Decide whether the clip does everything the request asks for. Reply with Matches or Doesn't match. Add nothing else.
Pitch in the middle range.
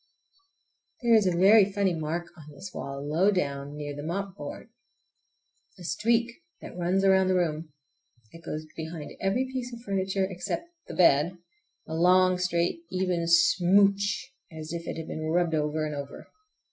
Matches